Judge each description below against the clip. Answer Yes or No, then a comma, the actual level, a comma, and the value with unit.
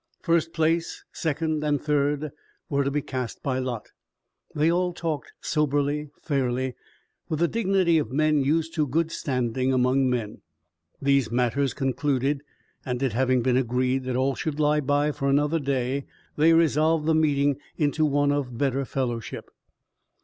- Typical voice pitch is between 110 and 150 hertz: Yes, medium, 140 Hz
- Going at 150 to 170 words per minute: Yes, average, 155 wpm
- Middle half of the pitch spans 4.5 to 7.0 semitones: No, average, 2.9 semitones